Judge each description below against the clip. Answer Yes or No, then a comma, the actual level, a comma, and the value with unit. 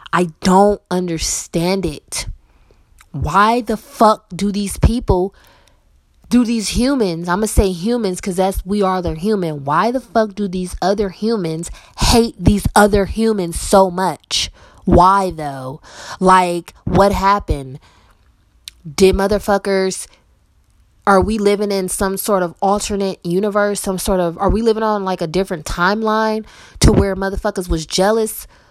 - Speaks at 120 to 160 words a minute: Yes, average, 145 wpm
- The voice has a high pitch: Yes, high, 195 Hz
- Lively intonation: No, narrow, 2.6 semitones